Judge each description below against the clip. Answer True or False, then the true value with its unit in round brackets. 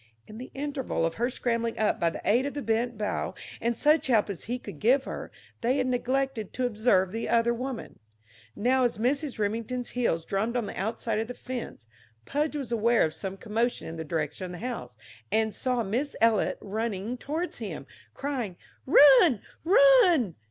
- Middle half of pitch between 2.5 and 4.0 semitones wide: True (3.7 semitones)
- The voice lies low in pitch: False (235 Hz)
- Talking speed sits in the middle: True (185 wpm)